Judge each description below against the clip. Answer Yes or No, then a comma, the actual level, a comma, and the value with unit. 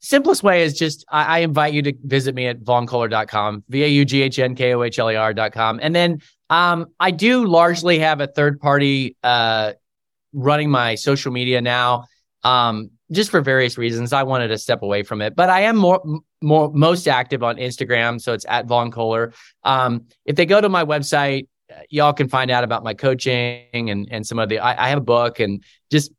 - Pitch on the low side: Yes, low, 130 Hz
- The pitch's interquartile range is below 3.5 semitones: No, average, 4.3 semitones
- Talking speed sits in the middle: Yes, average, 190 wpm